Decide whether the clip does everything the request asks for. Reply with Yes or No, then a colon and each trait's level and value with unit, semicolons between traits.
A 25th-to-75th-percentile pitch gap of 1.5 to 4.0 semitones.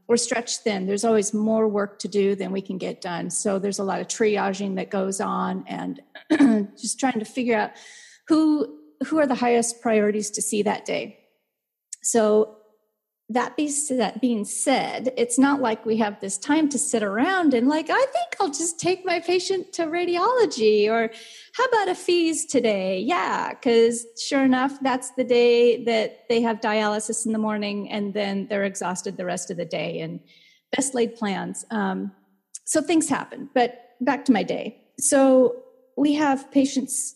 No: average, 4.5 semitones